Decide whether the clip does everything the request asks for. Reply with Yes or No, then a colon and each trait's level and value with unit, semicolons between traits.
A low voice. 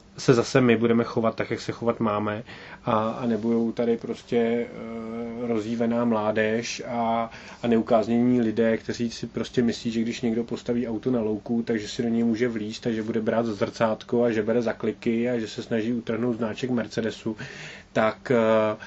Yes: low, 115 Hz